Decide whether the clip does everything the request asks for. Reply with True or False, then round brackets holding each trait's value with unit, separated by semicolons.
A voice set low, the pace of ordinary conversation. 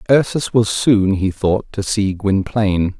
True (105 Hz; 160 wpm)